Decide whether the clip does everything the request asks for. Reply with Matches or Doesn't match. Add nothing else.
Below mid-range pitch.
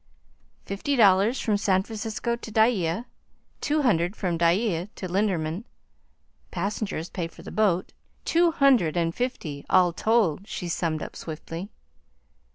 Doesn't match